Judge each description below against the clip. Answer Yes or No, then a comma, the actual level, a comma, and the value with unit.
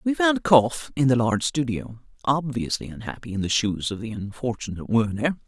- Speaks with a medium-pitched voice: No, low, 125 Hz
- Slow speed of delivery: No, average, 175 wpm